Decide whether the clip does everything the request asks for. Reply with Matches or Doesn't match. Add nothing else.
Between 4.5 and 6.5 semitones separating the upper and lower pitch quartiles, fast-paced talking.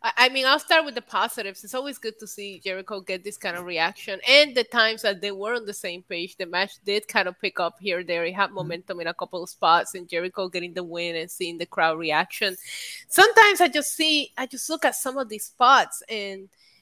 Matches